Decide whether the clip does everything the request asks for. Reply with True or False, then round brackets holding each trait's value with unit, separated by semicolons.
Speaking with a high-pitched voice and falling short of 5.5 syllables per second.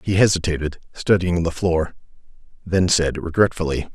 False (85 Hz; 5.0 syllables/s)